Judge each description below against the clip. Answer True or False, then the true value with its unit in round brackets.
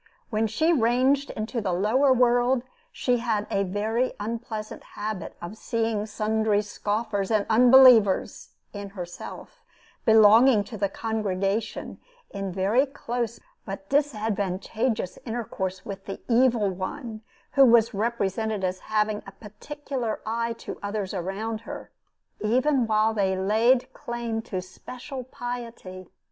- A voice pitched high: True (220 Hz)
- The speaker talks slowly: True (125 wpm)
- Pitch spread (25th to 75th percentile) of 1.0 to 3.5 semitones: True (3.0 semitones)